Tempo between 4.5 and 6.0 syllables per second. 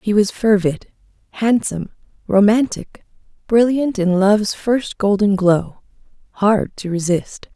No: 4.2 syllables/s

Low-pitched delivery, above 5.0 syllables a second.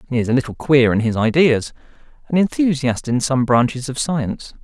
Yes: low, 130 Hz; 5.5 syllables/s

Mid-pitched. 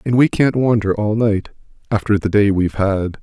No: low, 105 Hz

